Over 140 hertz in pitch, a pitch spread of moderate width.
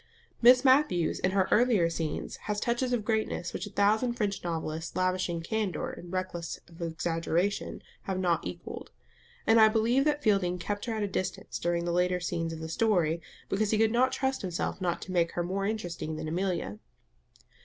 Yes: medium, 185 Hz; average, 4.3 semitones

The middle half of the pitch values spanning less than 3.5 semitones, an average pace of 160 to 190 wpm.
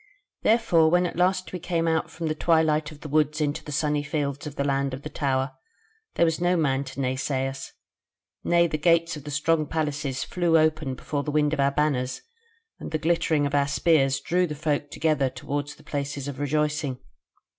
No: narrow, 2.5 semitones; fast, 205 wpm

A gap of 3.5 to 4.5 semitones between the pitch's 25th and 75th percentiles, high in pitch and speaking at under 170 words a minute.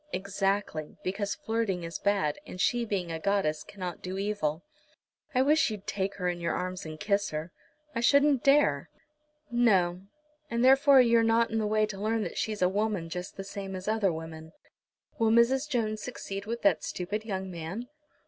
No: average, 3.9 semitones; high, 200 Hz; average, 185 wpm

